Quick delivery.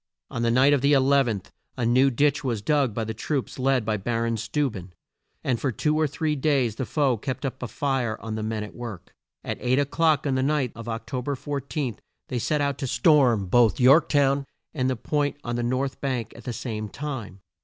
Yes: fast, 230 wpm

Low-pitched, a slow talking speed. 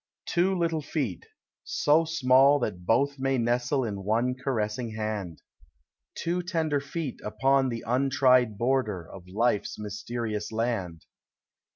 Yes: low, 125 Hz; slow, 130 wpm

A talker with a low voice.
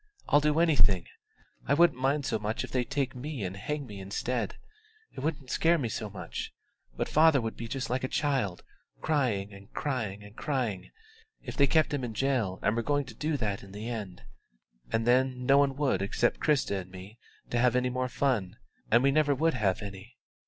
Yes: low, 125 Hz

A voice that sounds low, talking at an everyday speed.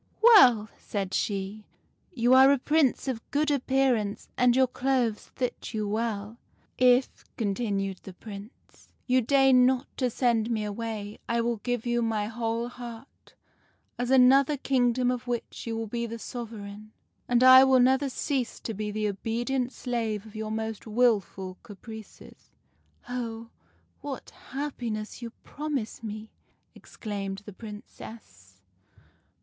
No: high, 235 Hz; average, 155 wpm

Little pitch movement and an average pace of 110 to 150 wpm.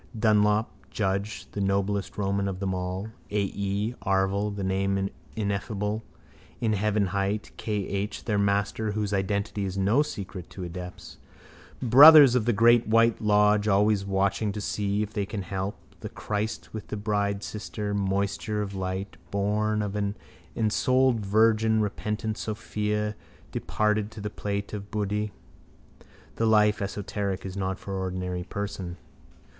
Yes: narrow, 1.5 semitones; average, 140 wpm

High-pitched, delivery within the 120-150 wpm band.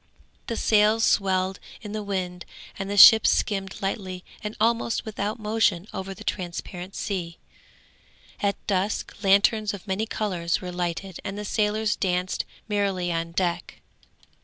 Yes: high, 195 Hz; average, 140 wpm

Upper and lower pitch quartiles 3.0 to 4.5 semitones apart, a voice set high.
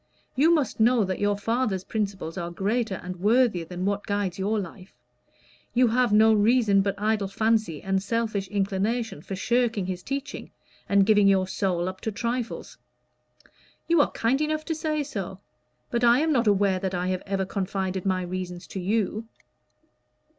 Yes: average, 3.6 semitones; high, 205 Hz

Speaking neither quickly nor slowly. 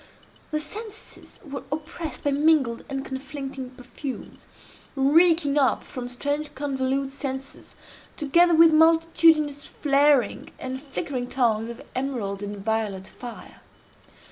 No: slow, 115 wpm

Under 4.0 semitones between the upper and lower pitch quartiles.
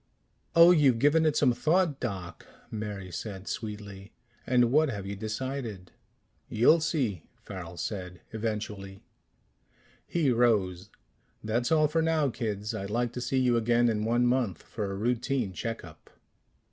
No: average, 4.7 semitones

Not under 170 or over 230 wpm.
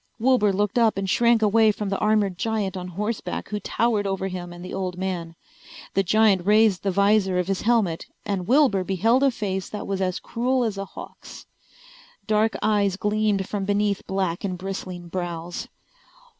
Yes: average, 180 wpm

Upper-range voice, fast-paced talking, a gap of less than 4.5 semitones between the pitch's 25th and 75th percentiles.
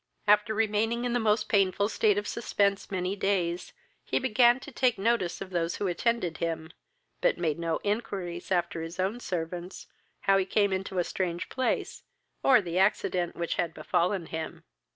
No: high, 195 Hz; average, 175 wpm; average, 3.6 semitones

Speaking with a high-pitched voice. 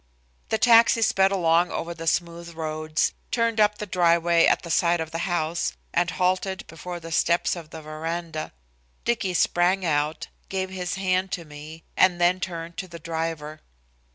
No: medium, 170 Hz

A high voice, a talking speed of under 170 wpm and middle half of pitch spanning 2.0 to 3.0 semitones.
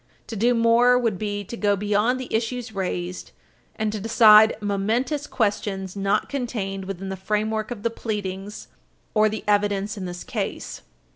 Yes: high, 210 Hz; average, 160 wpm; average, 2.7 semitones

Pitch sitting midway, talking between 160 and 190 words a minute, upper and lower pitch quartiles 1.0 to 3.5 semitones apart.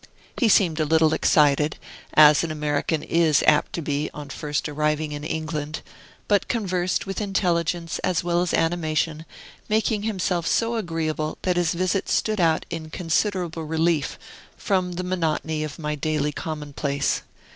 No: medium, 160 Hz; average, 150 wpm; average, 2.9 semitones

